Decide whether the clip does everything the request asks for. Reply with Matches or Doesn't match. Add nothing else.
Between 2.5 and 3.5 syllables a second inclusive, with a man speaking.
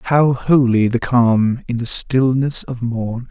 Matches